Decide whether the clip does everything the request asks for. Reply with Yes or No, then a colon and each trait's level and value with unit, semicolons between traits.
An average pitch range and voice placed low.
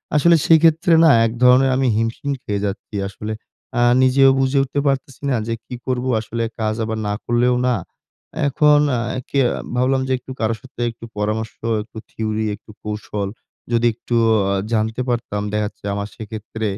Yes: average, 3.4 semitones; low, 115 Hz